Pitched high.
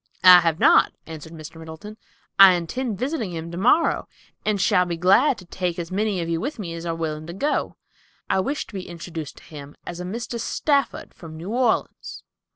No: medium, 180 Hz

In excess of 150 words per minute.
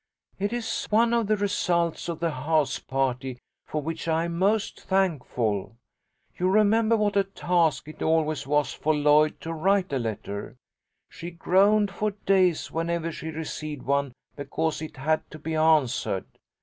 Yes: average, 160 wpm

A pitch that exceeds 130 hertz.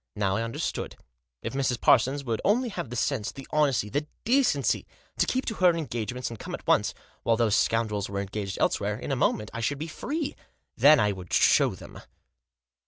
No: low, 125 Hz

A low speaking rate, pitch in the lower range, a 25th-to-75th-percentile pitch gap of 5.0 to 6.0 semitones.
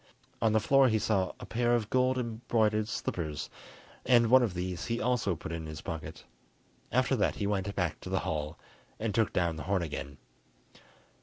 No: average, 185 wpm; low, 105 Hz; wide, 5.4 semitones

